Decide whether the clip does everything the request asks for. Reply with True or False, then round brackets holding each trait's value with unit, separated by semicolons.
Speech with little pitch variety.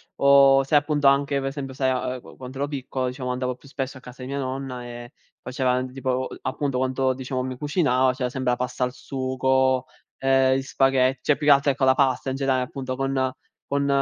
True (1.2 semitones)